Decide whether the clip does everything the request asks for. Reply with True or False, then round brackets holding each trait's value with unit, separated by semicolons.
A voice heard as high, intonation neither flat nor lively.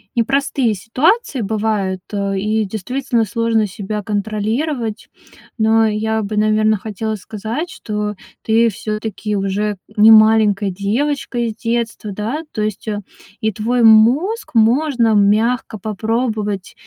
False (220 Hz; 1.9 semitones)